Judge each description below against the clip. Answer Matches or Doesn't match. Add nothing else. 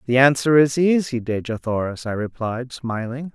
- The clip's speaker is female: Doesn't match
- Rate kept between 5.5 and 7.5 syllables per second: Doesn't match